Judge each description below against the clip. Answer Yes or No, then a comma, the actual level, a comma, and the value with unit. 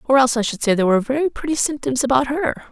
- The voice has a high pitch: Yes, very high, 255 Hz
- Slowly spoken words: No, fast, 265 wpm